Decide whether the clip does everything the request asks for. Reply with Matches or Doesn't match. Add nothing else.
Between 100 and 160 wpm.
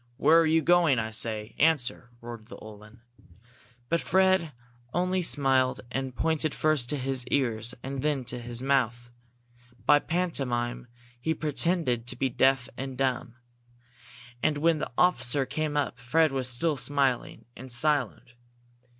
Matches